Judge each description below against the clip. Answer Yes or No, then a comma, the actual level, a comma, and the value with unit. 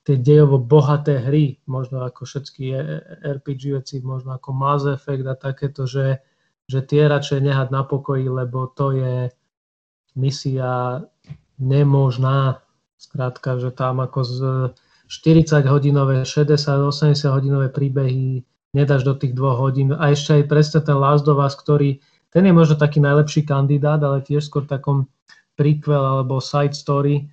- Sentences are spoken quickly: No, average, 145 wpm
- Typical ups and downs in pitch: No, narrow, 1.7 semitones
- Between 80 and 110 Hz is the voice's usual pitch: No, medium, 140 Hz